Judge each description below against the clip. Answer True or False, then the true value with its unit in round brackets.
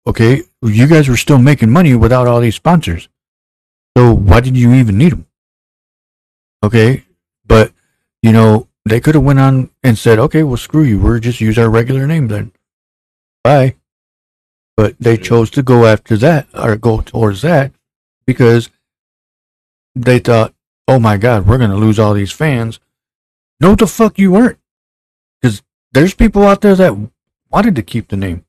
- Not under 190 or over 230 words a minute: False (170 wpm)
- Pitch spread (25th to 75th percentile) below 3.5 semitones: False (4.3 semitones)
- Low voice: True (115 Hz)